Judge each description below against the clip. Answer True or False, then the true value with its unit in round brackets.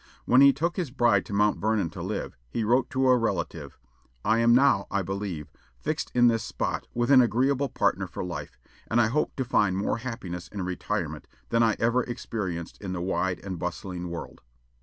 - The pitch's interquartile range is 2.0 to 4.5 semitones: False (4.9 semitones)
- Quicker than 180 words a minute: True (200 wpm)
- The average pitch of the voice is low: True (110 Hz)